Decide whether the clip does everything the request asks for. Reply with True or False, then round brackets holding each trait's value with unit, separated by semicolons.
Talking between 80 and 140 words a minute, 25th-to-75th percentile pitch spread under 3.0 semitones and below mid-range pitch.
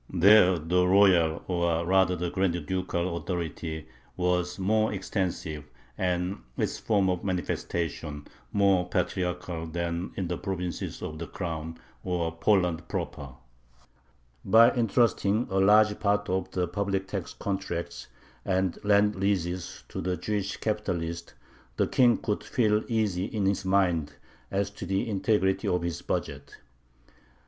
True (135 wpm; 2.5 semitones; 95 Hz)